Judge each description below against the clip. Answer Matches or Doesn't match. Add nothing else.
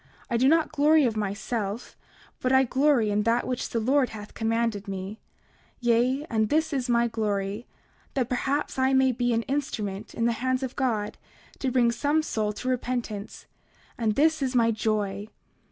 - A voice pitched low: Doesn't match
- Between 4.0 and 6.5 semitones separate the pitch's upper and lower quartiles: Doesn't match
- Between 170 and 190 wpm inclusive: Matches